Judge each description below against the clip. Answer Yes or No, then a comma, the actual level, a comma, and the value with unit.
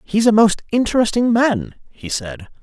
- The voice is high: Yes, high, 195 Hz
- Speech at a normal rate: Yes, average, 160 wpm